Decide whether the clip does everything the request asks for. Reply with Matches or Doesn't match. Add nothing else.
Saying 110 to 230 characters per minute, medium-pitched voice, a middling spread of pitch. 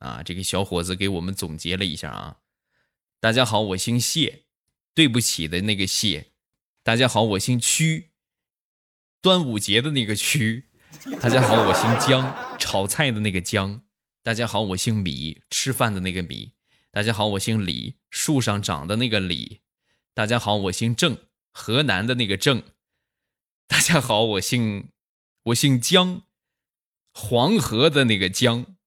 Doesn't match